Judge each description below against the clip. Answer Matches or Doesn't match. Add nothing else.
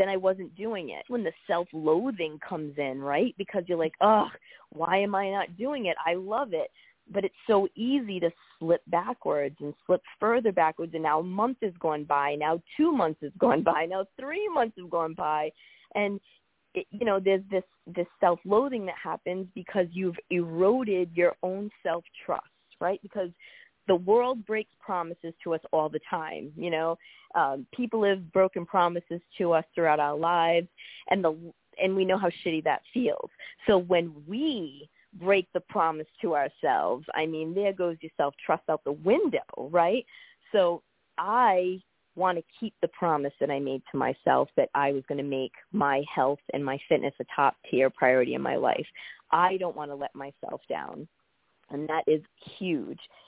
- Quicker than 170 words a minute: Matches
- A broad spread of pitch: Doesn't match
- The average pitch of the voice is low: Doesn't match